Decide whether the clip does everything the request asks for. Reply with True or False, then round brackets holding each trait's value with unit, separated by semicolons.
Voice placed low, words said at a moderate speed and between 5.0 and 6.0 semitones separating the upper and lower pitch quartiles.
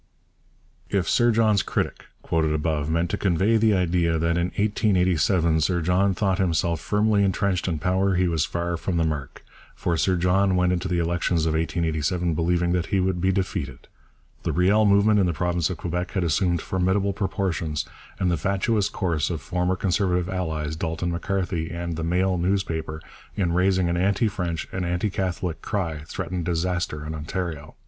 False (90 Hz; 175 wpm; 2.4 semitones)